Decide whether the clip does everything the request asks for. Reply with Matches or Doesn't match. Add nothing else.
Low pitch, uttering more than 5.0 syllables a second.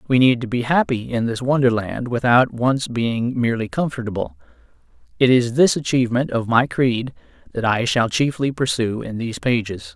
Matches